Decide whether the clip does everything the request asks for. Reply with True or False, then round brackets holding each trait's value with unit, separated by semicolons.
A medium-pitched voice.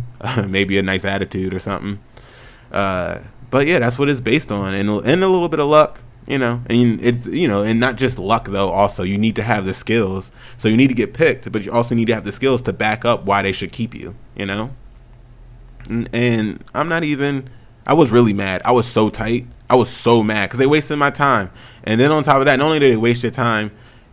False (120 Hz)